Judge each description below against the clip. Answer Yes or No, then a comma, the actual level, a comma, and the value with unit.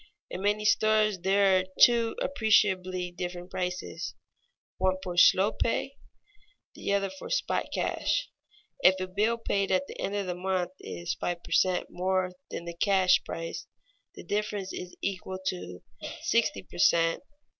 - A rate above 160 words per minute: No, average, 155 wpm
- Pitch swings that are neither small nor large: No, narrow, 2.1 semitones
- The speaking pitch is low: No, medium, 185 Hz